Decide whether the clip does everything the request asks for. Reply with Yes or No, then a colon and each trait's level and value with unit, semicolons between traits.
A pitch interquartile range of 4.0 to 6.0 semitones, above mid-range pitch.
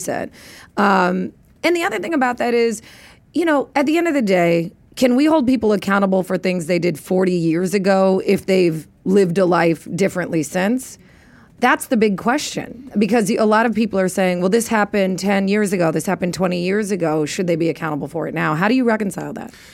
Yes: average, 4.5 semitones; high, 195 Hz